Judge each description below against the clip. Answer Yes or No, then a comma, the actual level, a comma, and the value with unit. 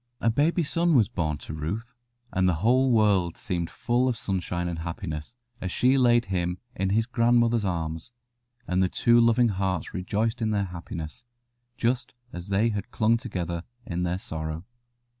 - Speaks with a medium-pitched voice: No, low, 100 Hz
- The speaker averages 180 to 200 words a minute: No, average, 170 wpm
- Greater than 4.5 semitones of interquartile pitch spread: Yes, average, 5.2 semitones